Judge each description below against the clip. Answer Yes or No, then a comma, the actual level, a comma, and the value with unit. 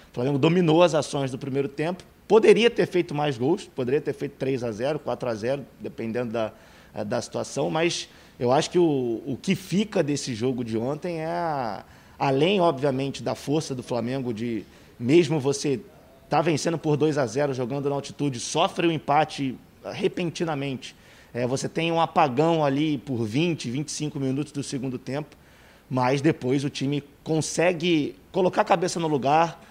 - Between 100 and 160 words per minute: No, average, 170 wpm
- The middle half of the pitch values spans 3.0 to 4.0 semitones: Yes, average, 3.7 semitones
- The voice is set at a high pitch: No, medium, 145 Hz